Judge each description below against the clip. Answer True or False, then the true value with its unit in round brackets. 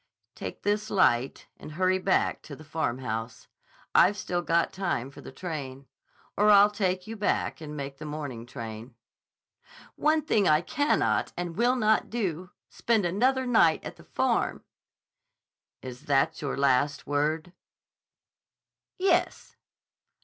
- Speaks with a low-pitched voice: False (165 Hz)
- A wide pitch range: True (6.8 semitones)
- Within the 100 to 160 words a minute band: True (135 wpm)